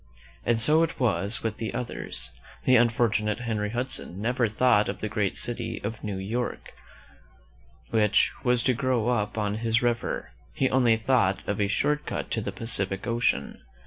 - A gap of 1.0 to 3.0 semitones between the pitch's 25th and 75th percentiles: Yes, average, 2.7 semitones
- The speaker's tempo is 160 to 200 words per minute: Yes, average, 170 wpm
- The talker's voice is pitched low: Yes, low, 115 Hz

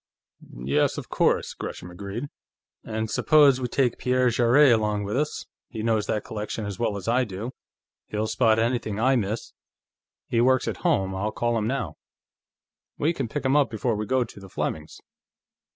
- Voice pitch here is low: Yes, low, 115 Hz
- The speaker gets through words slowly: No, average, 180 wpm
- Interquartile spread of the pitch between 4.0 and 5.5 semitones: No, average, 3.3 semitones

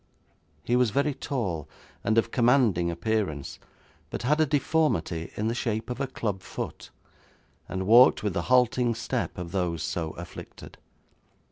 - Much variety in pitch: Yes, wide, 6.1 semitones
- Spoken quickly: No, average, 150 wpm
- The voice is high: No, low, 110 Hz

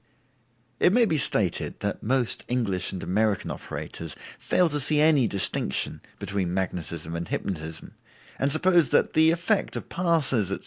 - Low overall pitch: Yes, low, 120 Hz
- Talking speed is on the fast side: No, average, 150 wpm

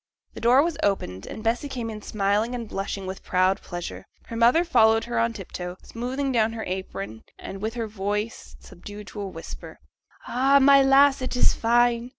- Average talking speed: Yes, average, 190 wpm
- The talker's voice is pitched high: Yes, high, 225 Hz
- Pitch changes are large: No, average, 3.9 semitones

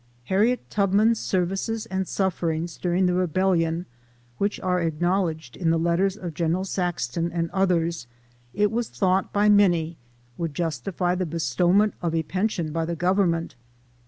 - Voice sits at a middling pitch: Yes, medium, 180 Hz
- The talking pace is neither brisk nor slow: Yes, average, 145 wpm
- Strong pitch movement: No, narrow, 2.6 semitones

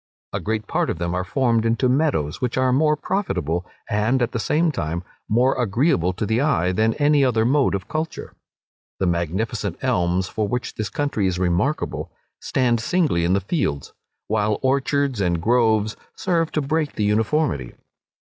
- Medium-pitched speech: No, low, 110 Hz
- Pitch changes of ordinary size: No, wide, 7.0 semitones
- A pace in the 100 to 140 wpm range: No, average, 170 wpm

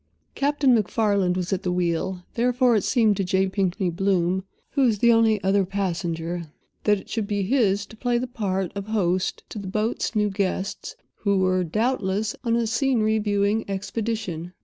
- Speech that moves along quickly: No, average, 175 wpm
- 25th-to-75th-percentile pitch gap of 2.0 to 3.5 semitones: Yes, average, 3.1 semitones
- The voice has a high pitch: Yes, high, 200 Hz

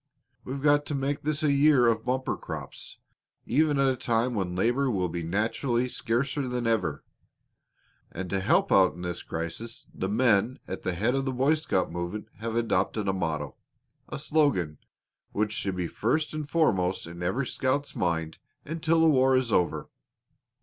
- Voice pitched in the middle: No, low, 115 Hz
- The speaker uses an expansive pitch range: Yes, wide, 6.8 semitones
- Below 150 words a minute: No, average, 175 wpm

